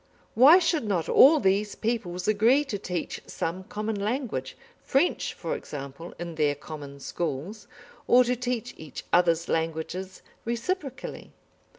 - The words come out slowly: Yes, slow, 130 wpm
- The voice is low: No, high, 200 Hz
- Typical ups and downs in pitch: No, wide, 7.1 semitones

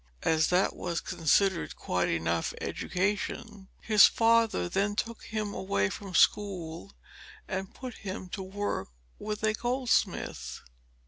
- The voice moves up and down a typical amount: Yes, average, 4.0 semitones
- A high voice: Yes, high, 195 Hz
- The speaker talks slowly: Yes, slow, 125 wpm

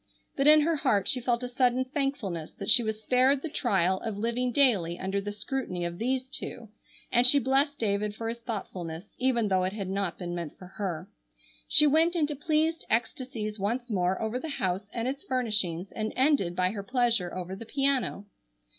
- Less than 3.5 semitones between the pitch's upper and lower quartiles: No, average, 5.3 semitones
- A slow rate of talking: No, average, 195 wpm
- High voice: Yes, high, 230 Hz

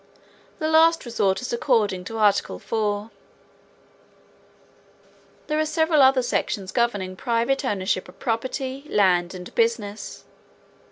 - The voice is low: No, high, 230 Hz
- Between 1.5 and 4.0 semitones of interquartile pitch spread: No, average, 5.0 semitones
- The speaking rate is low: Yes, slow, 115 wpm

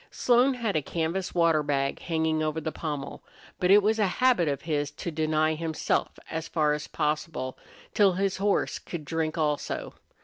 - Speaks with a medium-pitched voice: Yes, medium, 160 Hz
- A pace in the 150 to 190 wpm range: Yes, average, 175 wpm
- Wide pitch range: No, average, 3.3 semitones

